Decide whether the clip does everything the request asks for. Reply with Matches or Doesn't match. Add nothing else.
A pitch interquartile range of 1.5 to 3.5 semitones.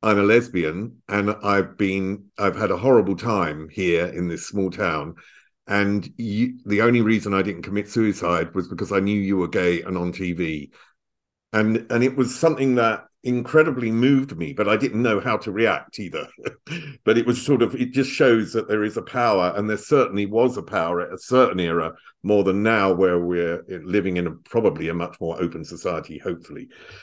Doesn't match